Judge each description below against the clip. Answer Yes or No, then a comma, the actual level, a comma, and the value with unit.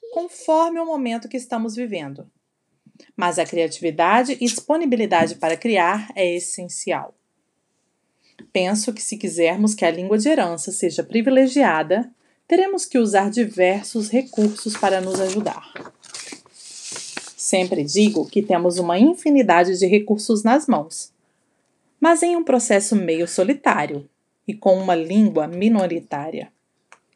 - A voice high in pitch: Yes, high, 210 Hz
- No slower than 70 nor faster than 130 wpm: Yes, slow, 120 wpm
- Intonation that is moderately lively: No, wide, 5.7 semitones